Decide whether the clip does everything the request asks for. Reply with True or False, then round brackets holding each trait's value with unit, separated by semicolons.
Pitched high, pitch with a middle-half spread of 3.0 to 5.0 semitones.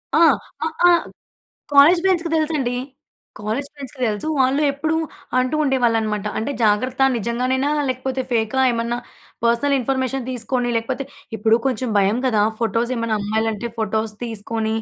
True (245 Hz; 3.3 semitones)